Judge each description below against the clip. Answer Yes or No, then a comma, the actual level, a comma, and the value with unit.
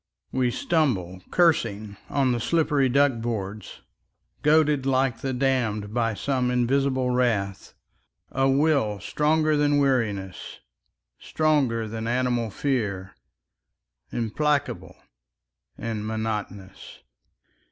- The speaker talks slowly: Yes, slow, 95 wpm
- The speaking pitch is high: No, low, 125 Hz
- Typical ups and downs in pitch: Yes, average, 4.3 semitones